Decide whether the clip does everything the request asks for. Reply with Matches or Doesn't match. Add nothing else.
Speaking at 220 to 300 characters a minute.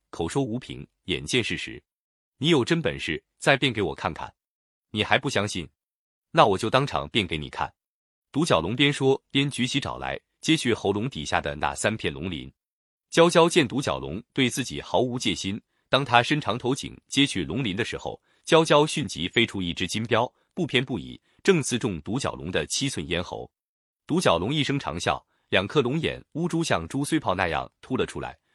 Matches